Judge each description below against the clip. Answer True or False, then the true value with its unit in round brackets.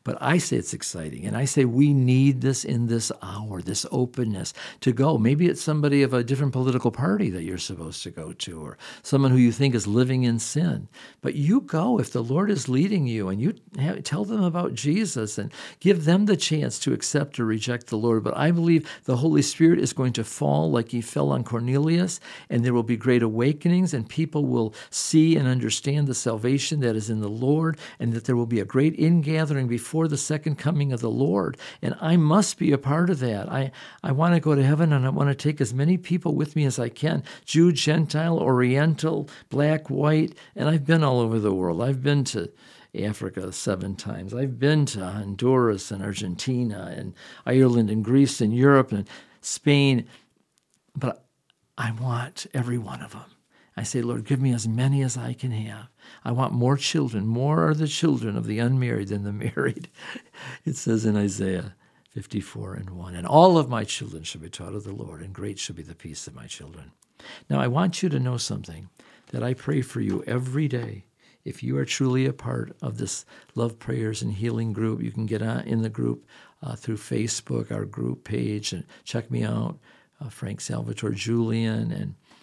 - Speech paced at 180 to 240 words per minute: True (205 wpm)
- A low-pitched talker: True (125 Hz)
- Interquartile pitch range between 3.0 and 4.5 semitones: False (5.1 semitones)